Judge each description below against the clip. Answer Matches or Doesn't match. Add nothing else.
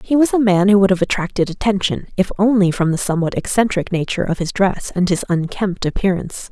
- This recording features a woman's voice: Matches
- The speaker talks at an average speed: Doesn't match